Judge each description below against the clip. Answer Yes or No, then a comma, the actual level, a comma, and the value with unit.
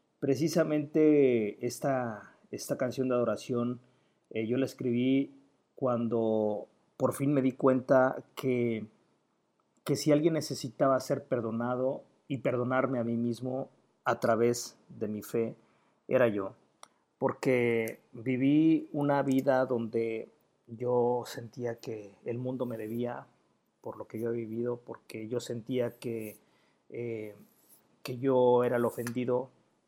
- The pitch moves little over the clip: Yes, narrow, 2.3 semitones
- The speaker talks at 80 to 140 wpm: Yes, slow, 125 wpm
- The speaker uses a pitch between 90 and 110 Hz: No, low, 125 Hz